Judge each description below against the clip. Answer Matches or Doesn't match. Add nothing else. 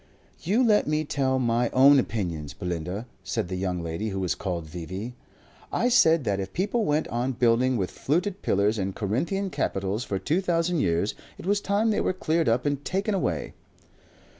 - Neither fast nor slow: Matches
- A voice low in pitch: Matches